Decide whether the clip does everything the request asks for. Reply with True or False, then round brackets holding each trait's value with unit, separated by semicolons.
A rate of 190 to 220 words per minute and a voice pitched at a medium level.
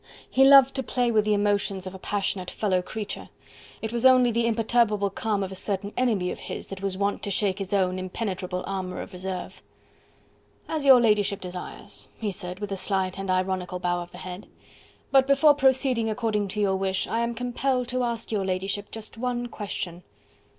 False (195 wpm; 205 Hz)